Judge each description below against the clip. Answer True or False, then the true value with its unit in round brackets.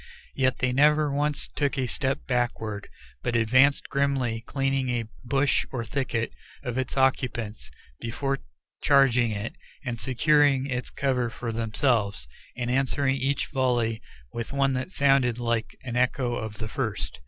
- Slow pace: False (145 wpm)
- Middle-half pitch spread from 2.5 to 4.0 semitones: True (2.8 semitones)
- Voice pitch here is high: False (125 Hz)